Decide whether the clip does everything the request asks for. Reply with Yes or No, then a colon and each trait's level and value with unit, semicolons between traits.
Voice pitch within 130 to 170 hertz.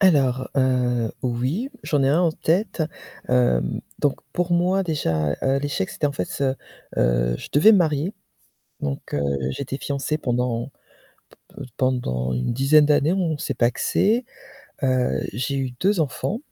Yes: low, 135 Hz